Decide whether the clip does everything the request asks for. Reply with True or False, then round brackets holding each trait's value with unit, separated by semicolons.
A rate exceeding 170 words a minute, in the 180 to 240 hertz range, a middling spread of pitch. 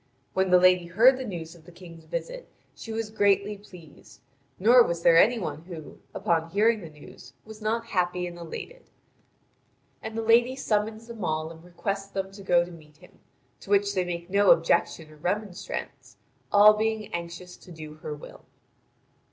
True (180 wpm; 190 Hz; 4.4 semitones)